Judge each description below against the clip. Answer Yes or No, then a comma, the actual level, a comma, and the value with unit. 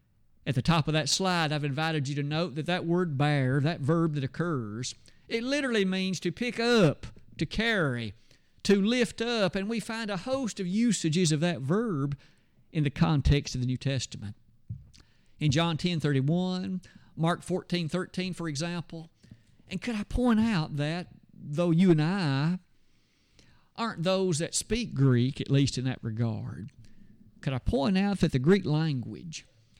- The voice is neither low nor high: Yes, medium, 165 Hz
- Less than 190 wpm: Yes, average, 170 wpm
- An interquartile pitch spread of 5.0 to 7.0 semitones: Yes, wide, 5.4 semitones